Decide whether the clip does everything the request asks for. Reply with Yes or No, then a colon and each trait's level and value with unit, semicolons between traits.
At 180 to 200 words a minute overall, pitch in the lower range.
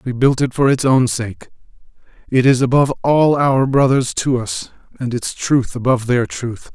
Yes: average, 185 wpm; low, 125 Hz